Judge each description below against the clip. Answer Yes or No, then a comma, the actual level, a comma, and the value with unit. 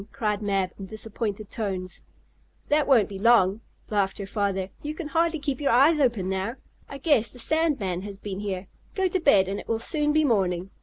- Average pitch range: No, wide, 6.6 semitones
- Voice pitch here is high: Yes, high, 215 Hz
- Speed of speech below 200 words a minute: No, fast, 205 wpm